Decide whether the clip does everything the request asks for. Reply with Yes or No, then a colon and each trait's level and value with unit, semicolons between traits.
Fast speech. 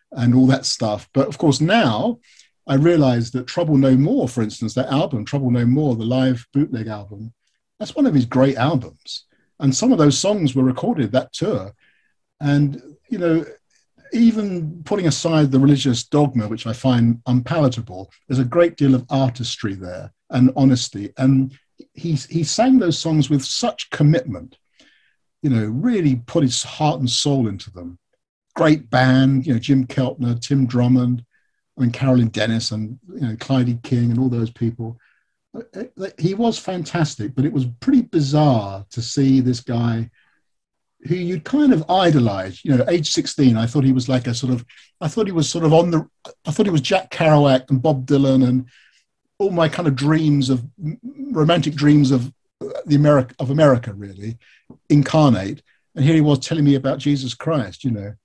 No: average, 180 wpm